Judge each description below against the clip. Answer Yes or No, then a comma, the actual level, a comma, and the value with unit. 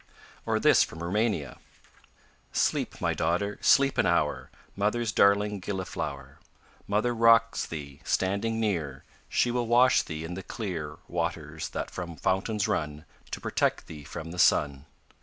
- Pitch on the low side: Yes, very low, 95 Hz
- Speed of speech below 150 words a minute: Yes, average, 140 wpm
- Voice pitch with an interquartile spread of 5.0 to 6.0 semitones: Yes, wide, 5.6 semitones